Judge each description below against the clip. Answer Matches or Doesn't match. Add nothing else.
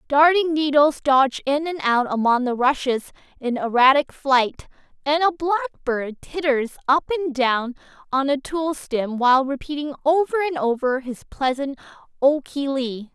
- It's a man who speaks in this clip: Doesn't match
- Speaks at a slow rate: Doesn't match